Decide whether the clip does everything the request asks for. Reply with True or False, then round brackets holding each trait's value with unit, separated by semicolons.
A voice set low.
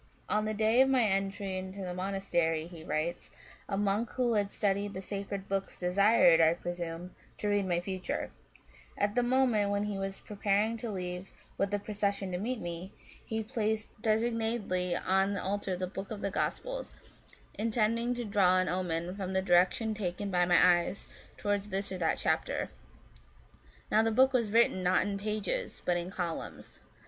False (200 Hz)